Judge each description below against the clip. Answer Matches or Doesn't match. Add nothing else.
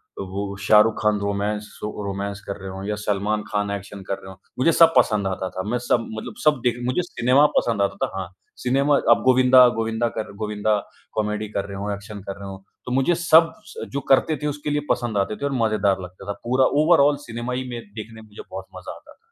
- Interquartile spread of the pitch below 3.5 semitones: Doesn't match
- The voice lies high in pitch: Doesn't match